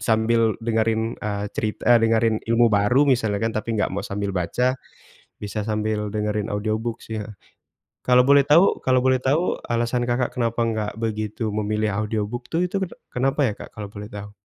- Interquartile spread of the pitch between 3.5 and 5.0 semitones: No, narrow, 2.4 semitones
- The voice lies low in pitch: Yes, low, 110 Hz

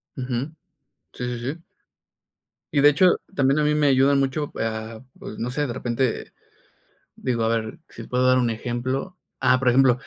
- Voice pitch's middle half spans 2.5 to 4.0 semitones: Yes, average, 2.8 semitones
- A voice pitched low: Yes, low, 130 Hz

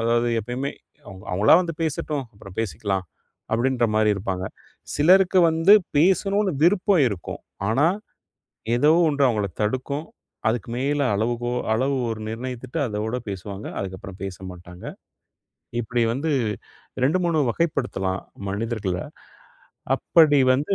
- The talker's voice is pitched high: No, low, 120 Hz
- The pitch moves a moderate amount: No, wide, 6.2 semitones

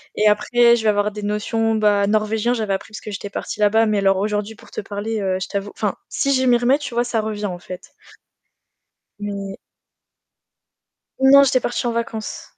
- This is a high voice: Yes, high, 215 Hz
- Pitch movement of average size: No, narrow, 2.3 semitones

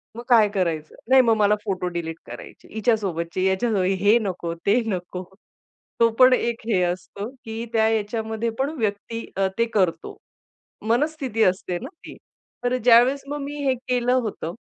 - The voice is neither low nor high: No, high, 220 Hz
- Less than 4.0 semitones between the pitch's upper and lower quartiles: No, average, 4.3 semitones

